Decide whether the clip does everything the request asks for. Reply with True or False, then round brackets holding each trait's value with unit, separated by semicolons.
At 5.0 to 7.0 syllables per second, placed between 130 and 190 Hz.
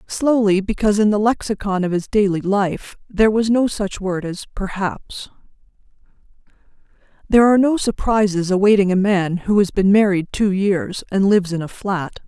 False (5.1 syllables/s; 200 Hz)